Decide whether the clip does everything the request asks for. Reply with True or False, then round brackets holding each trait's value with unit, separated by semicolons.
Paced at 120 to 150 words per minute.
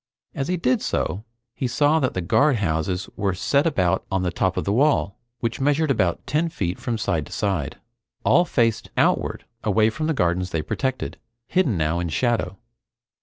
False (180 wpm)